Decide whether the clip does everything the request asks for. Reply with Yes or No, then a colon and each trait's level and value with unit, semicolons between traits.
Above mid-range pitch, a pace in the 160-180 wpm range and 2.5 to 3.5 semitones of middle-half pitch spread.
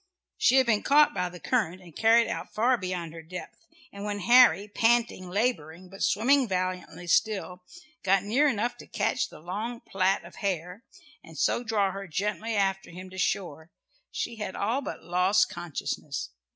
No: high, 195 Hz; average, 175 wpm; average, 4.0 semitones